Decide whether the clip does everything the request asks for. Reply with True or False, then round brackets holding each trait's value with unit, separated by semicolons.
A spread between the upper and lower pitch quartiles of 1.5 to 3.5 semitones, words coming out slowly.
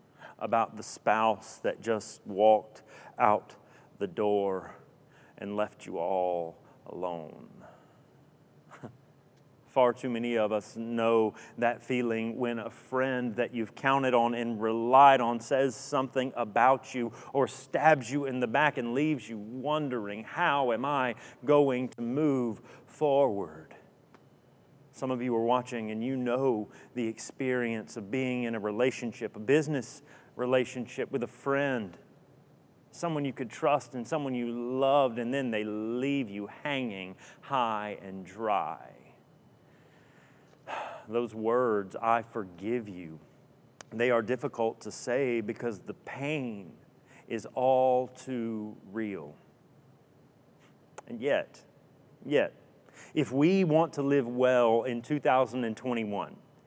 True (2.9 semitones; 125 wpm)